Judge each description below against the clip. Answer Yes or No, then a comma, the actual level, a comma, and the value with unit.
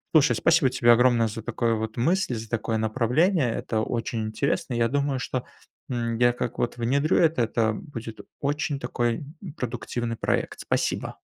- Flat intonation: No, average, 3.3 semitones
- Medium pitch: No, low, 120 Hz